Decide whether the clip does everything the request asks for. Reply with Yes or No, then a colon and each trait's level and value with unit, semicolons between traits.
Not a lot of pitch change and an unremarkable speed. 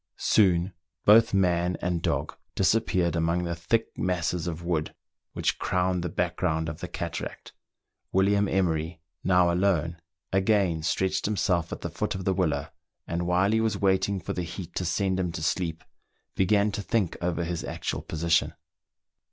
Yes: narrow, 2.2 semitones; average, 165 wpm